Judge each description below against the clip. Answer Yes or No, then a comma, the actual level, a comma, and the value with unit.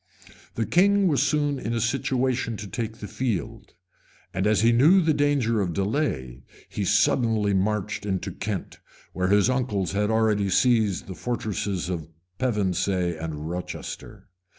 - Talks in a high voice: No, low, 105 Hz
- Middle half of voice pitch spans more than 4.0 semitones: Yes, average, 4.7 semitones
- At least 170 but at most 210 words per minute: No, average, 150 wpm